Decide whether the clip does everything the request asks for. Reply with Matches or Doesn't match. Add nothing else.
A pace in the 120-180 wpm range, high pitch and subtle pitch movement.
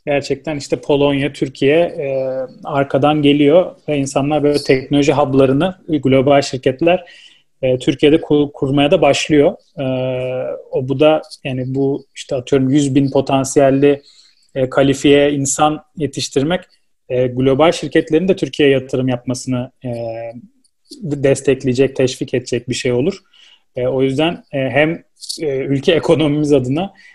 Doesn't match